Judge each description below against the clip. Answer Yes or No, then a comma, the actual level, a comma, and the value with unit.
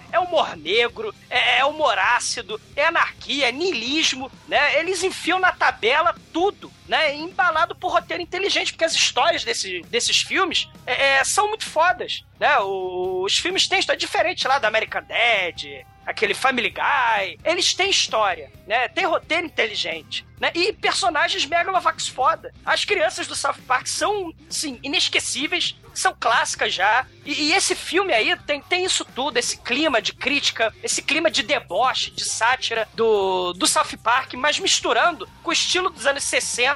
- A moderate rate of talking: Yes, average, 165 wpm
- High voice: Yes, very high, 325 Hz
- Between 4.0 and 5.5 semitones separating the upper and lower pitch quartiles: Yes, average, 5.1 semitones